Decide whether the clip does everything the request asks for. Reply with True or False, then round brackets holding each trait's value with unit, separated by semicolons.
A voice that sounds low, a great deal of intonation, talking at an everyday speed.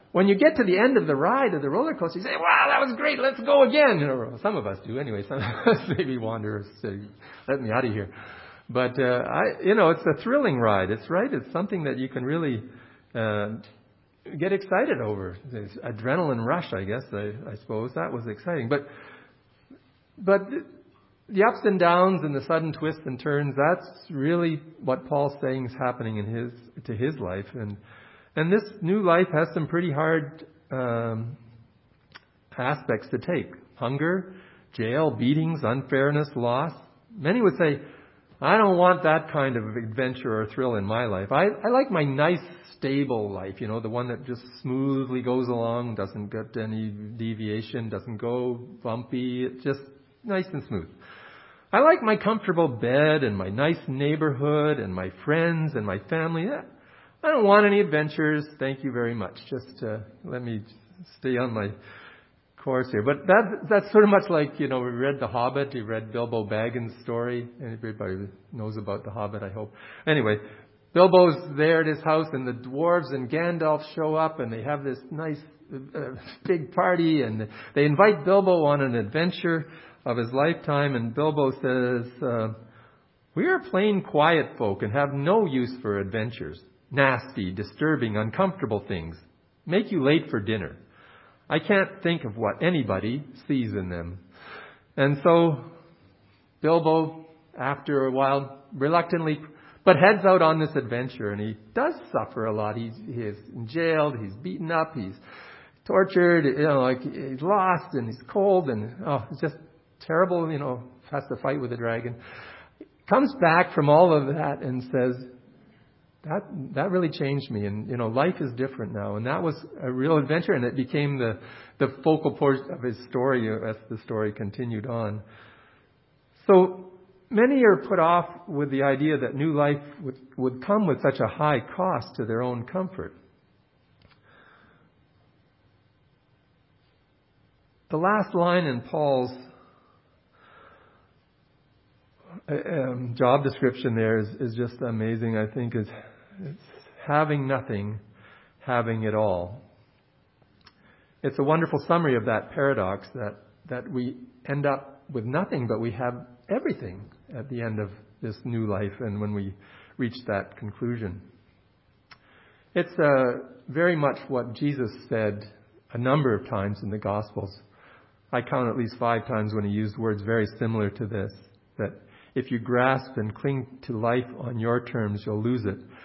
True (130 Hz; 5.8 semitones; 165 wpm)